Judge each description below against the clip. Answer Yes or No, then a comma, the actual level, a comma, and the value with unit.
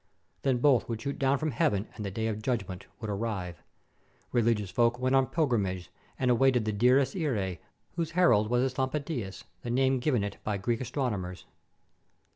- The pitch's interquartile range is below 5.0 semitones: Yes, average, 4.4 semitones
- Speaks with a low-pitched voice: Yes, low, 120 Hz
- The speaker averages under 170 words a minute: No, average, 180 wpm